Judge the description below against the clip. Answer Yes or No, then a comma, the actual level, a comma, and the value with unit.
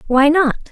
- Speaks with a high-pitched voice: Yes, very high, 290 Hz